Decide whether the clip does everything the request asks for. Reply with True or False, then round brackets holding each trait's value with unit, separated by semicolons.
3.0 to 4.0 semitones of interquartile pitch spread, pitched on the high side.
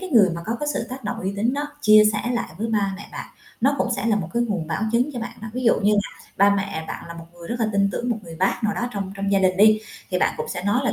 True (3.5 semitones; 205 Hz)